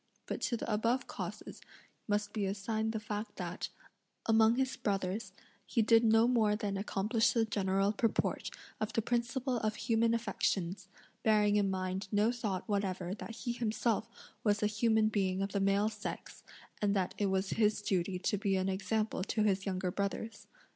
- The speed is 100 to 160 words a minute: No, average, 175 wpm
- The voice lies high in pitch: Yes, high, 210 Hz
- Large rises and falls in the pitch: No, narrow, 2.4 semitones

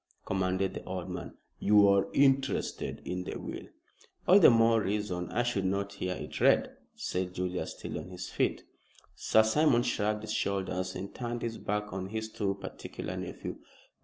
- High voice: No, low, 100 Hz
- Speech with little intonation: No, average, 3.2 semitones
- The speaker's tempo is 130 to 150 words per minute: No, average, 170 wpm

